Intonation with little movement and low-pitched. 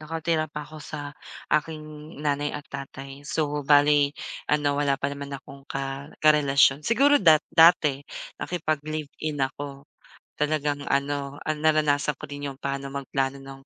No: narrow, 1.7 semitones; medium, 145 Hz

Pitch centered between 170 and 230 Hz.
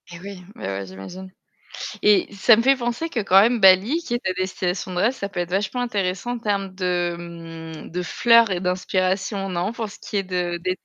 Yes: high, 190 Hz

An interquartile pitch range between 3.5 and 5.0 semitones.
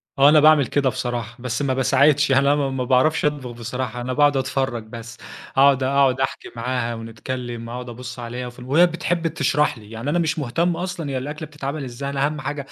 No: average, 3.0 semitones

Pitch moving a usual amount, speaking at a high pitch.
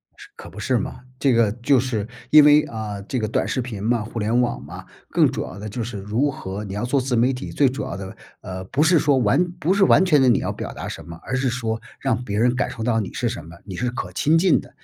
No: average, 4.1 semitones; low, 120 Hz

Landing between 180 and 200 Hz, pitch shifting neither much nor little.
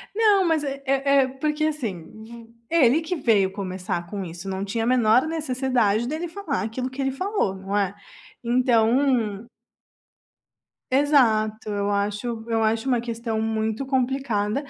No: high, 240 Hz; average, 4.5 semitones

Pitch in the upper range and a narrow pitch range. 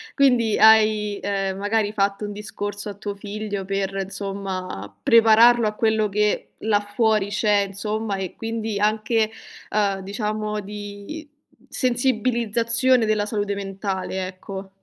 Yes: high, 210 Hz; narrow, 1.7 semitones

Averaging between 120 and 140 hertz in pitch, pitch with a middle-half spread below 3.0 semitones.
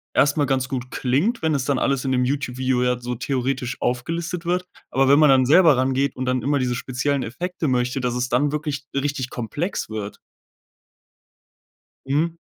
Yes: low, 135 Hz; narrow, 2.6 semitones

